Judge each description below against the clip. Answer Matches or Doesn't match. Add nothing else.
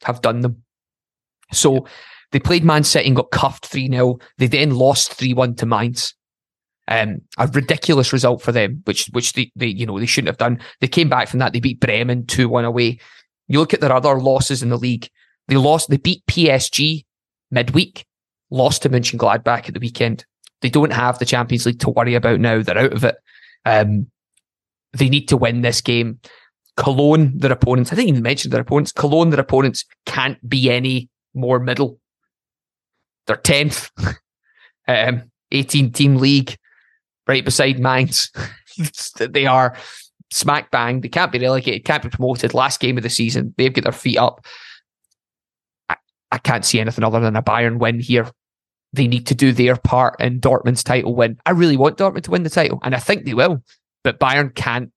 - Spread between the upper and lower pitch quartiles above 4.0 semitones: Doesn't match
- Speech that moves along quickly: Doesn't match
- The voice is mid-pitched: Doesn't match